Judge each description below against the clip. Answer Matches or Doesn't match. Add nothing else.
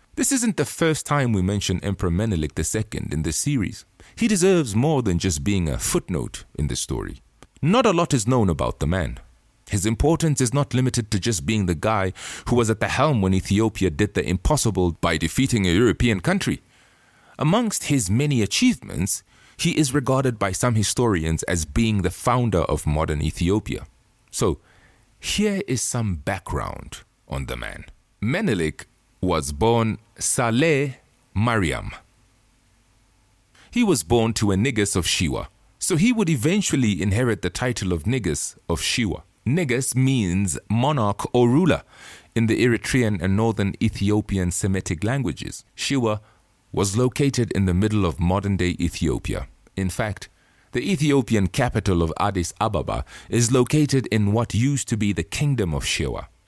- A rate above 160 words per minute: Doesn't match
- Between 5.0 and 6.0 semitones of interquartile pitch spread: Matches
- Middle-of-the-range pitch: Doesn't match